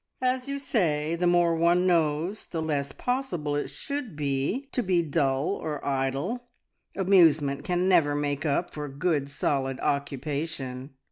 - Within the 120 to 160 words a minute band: Yes, average, 145 wpm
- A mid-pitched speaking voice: Yes, medium, 155 Hz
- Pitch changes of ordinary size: Yes, average, 4.3 semitones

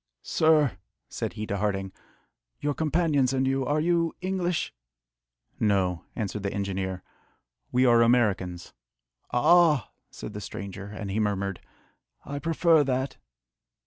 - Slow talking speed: Yes, slow, 125 wpm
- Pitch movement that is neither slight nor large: No, wide, 7.2 semitones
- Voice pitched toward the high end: No, low, 120 Hz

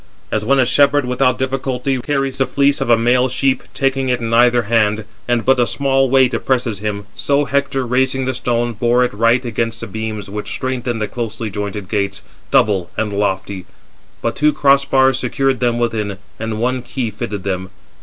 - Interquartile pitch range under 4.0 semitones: Yes, average, 3.4 semitones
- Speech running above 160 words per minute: Yes, average, 190 wpm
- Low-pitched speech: Yes, low, 120 Hz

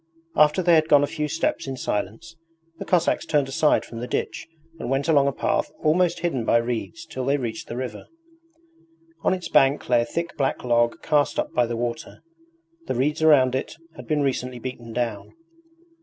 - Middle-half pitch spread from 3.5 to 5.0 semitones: Yes, average, 4.2 semitones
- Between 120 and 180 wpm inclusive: No, average, 195 wpm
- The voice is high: No, low, 135 Hz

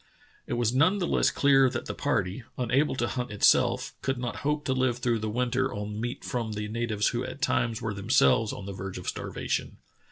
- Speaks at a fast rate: Yes, fast, 215 wpm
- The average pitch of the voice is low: Yes, low, 120 Hz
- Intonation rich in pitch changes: No, average, 3.4 semitones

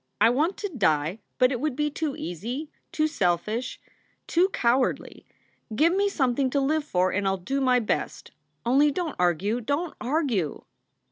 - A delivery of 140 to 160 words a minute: No, average, 180 wpm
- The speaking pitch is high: Yes, very high, 255 Hz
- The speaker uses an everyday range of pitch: No, wide, 6.7 semitones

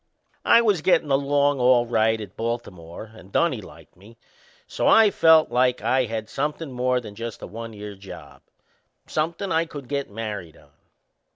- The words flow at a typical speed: Yes, average, 170 wpm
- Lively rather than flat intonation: No, average, 4.9 semitones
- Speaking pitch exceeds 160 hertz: No, low, 120 Hz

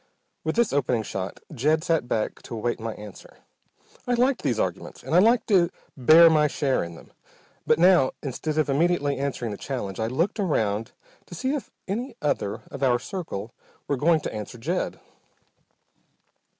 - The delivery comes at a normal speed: Yes, average, 175 wpm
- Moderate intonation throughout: No, wide, 6.6 semitones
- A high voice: No, medium, 145 Hz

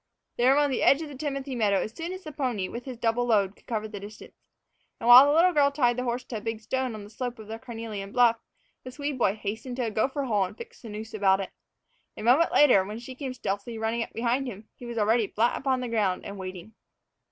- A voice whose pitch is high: Yes, high, 235 Hz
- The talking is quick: Yes, fast, 260 wpm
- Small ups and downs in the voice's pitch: No, average, 3.5 semitones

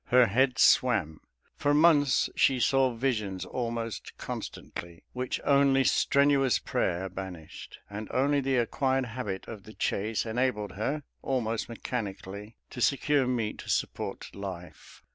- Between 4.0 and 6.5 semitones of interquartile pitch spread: Yes, average, 4.6 semitones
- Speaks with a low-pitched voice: Yes, low, 120 Hz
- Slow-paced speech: Yes, slow, 130 wpm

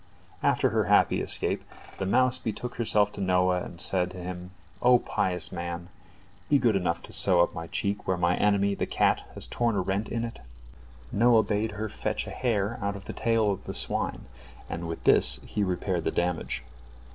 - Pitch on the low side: Yes, low, 100 Hz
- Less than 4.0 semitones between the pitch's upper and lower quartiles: Yes, average, 3.5 semitones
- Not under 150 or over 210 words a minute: Yes, average, 195 wpm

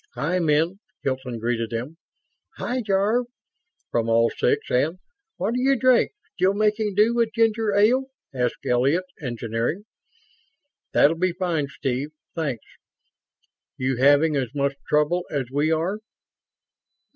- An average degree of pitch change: No, wide, 7.7 semitones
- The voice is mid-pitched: Yes, medium, 160 Hz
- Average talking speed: No, slow, 125 wpm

